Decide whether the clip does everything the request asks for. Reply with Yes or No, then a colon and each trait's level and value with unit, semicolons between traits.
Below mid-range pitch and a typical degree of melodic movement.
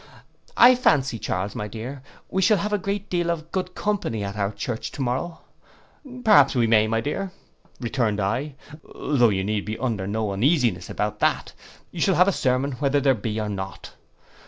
No: low, 130 Hz; wide, 8.2 semitones